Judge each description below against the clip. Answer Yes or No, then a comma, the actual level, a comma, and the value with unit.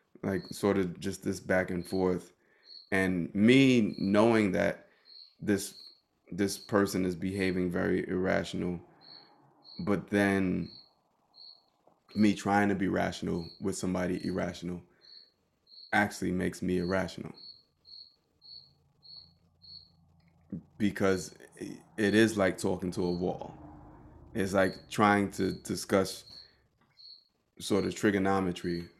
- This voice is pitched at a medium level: No, very low, 95 Hz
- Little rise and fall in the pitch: Yes, narrow, 2.1 semitones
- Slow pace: Yes, slow, 100 wpm